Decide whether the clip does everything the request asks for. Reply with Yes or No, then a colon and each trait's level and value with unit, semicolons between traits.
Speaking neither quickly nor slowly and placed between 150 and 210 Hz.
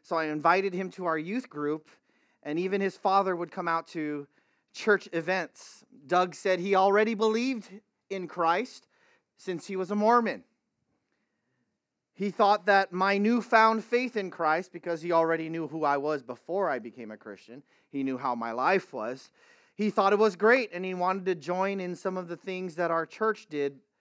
Yes: average, 185 wpm; medium, 185 Hz